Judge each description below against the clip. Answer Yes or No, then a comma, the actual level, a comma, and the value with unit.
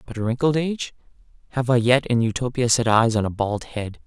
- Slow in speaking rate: No, fast, 205 wpm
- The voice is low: Yes, low, 120 Hz